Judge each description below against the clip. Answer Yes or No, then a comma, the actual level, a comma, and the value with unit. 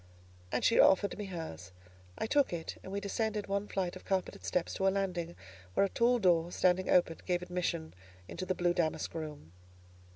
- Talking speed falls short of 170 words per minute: No, average, 190 wpm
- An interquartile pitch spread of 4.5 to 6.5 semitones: No, narrow, 2.6 semitones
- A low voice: No, medium, 180 Hz